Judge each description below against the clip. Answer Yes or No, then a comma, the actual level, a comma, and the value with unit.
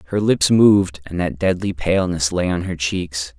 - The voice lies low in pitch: Yes, very low, 85 Hz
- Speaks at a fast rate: No, average, 195 wpm